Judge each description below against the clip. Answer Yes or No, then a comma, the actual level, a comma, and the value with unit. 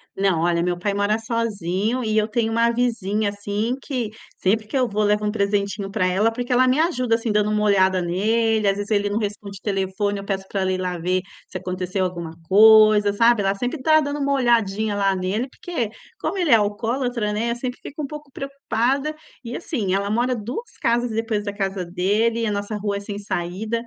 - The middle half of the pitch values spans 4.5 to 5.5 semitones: No, average, 3.0 semitones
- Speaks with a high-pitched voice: Yes, high, 210 Hz